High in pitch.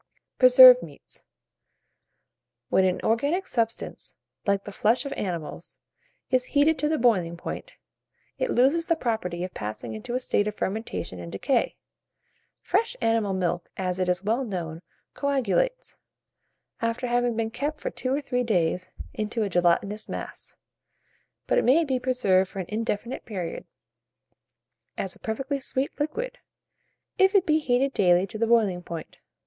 Yes: high, 230 Hz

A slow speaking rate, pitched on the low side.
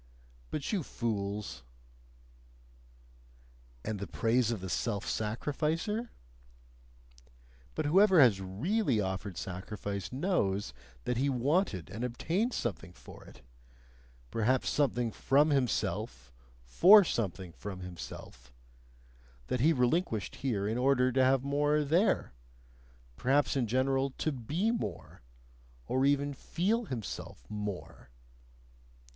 Yes: slow, 110 wpm; low, 125 Hz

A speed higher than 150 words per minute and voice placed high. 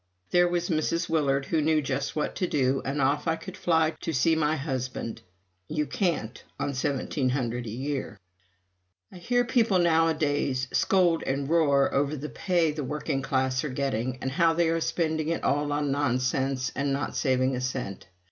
No: average, 175 wpm; medium, 145 Hz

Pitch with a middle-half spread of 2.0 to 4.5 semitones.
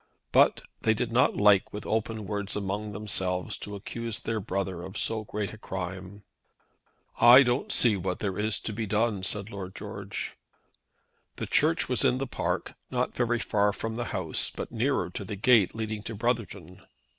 Yes: average, 2.7 semitones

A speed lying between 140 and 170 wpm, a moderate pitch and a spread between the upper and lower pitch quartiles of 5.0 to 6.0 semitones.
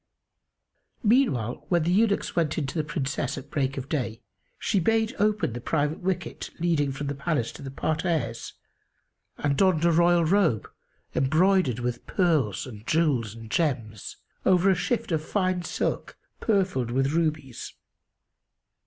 Yes: average, 150 wpm; medium, 155 Hz; average, 5.3 semitones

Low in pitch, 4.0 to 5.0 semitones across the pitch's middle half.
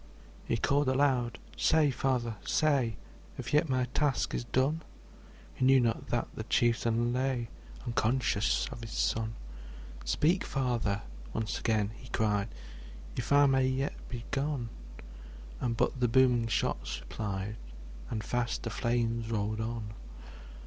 No: low, 120 Hz; average, 2.8 semitones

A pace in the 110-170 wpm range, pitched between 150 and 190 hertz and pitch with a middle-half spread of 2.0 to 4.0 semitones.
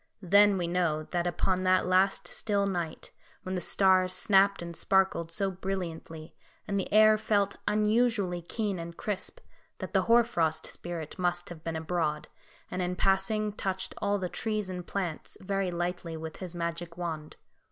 Yes: average, 165 wpm; medium, 185 Hz; narrow, 2.6 semitones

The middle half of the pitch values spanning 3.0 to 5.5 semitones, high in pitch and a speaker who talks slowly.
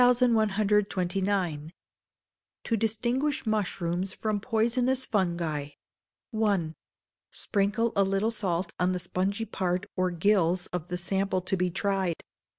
Yes: average, 3.4 semitones; high, 195 Hz; slow, 110 wpm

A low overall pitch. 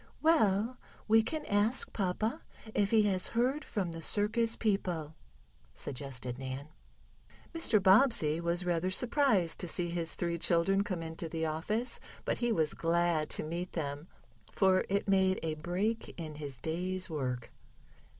No: medium, 180 Hz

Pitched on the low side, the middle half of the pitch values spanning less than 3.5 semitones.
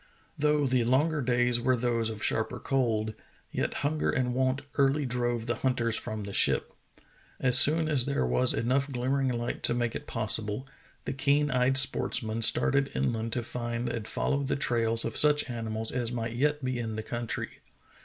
Yes: low, 125 Hz; average, 2.8 semitones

